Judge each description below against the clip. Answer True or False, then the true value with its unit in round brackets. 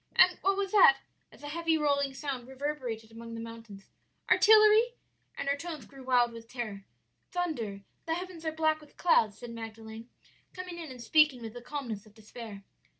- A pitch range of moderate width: False (6.0 semitones)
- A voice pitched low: False (265 Hz)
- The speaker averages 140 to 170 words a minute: False (180 wpm)